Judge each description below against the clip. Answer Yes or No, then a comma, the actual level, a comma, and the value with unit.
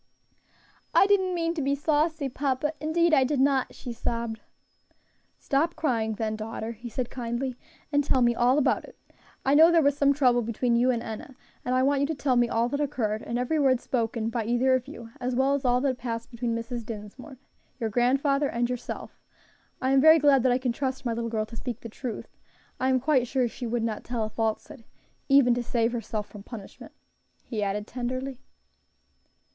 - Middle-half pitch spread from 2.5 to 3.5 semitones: Yes, average, 3.1 semitones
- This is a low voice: No, very high, 250 Hz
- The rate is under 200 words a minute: No, fast, 205 wpm